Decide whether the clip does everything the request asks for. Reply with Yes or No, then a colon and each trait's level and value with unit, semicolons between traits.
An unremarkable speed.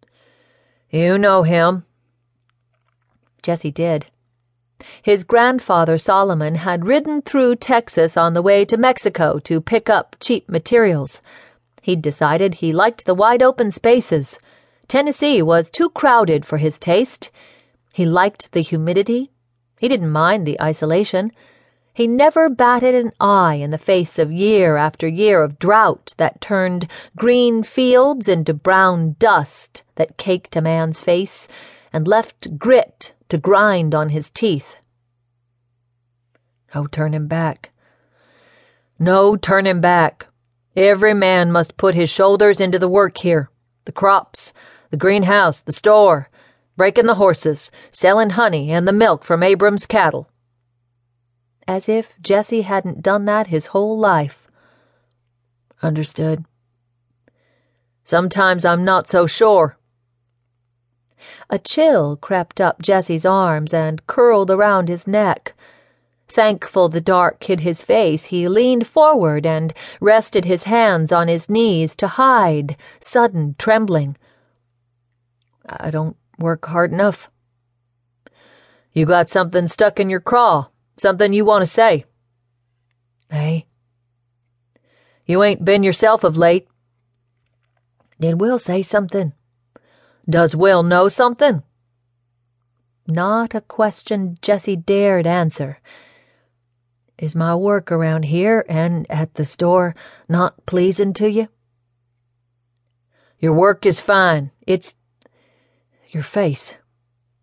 No: slow, 125 wpm